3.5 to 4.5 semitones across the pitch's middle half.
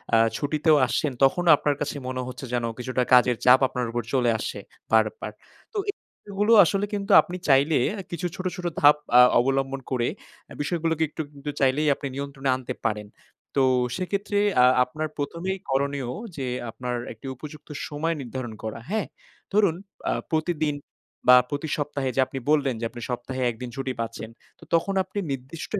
Yes: average, 4.1 semitones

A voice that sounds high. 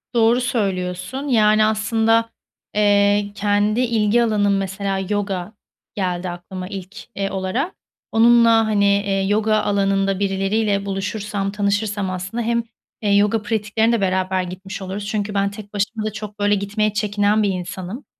Yes: high, 205 Hz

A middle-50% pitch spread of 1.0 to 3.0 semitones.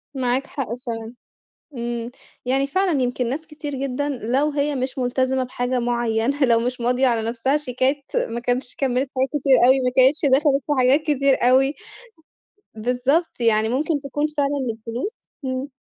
Yes: narrow, 2.4 semitones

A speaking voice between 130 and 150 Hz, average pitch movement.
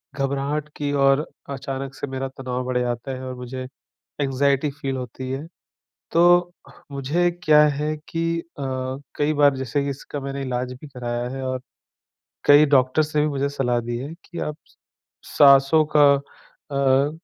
No: medium, 140 Hz; narrow, 2.2 semitones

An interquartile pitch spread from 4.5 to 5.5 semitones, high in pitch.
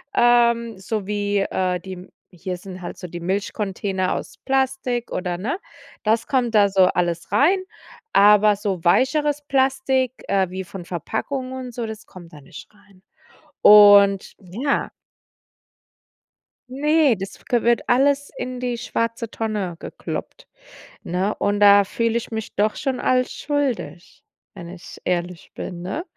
Yes: average, 5.1 semitones; high, 210 Hz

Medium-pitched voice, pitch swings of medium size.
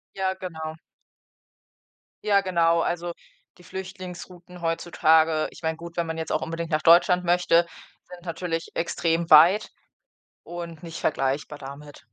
No: medium, 170 Hz; narrow, 1.7 semitones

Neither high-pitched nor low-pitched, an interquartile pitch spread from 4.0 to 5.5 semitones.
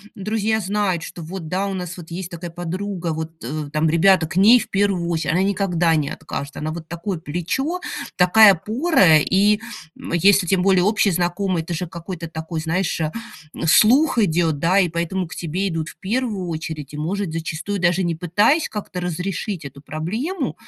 No: medium, 180 Hz; average, 3.4 semitones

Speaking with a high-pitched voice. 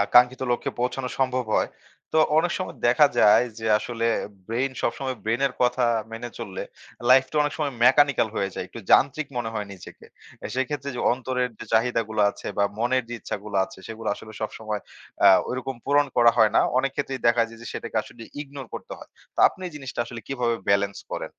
No: low, 125 Hz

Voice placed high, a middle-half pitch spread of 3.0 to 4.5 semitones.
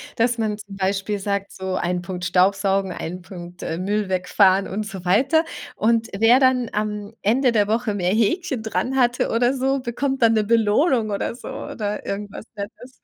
Yes: high, 210 Hz; average, 3.5 semitones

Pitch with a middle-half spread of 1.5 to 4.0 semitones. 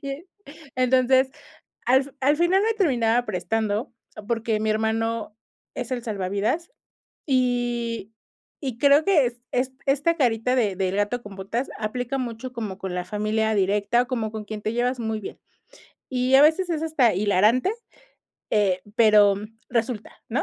Yes: average, 3.5 semitones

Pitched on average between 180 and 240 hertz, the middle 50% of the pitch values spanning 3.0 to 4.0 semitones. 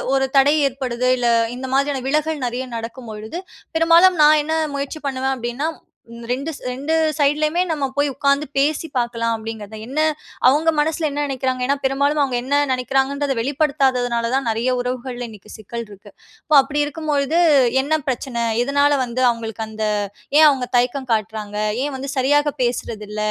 No: very high, 265 Hz; average, 3.4 semitones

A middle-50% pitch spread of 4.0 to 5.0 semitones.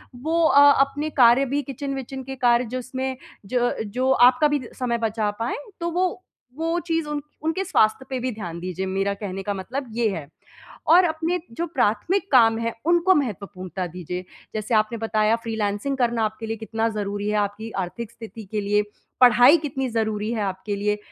Yes: average, 4.7 semitones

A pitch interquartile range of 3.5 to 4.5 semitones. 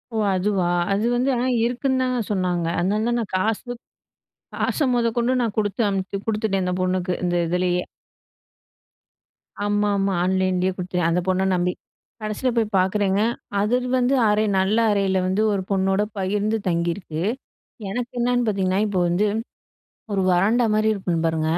No: average, 3.0 semitones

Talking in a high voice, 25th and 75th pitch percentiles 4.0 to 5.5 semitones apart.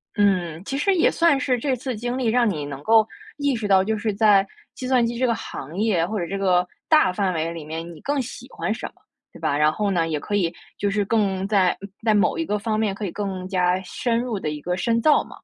Yes: high, 205 Hz; average, 4.5 semitones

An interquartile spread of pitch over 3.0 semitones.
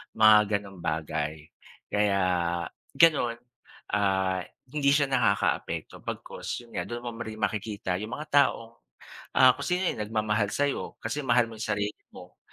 Yes: average, 3.6 semitones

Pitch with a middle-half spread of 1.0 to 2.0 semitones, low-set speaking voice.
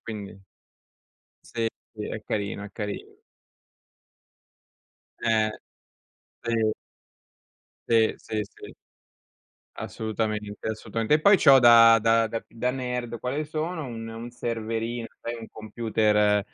Yes: narrow, 1.7 semitones; low, 115 Hz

